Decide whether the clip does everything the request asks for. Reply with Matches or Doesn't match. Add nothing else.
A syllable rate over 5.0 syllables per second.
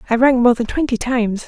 Matches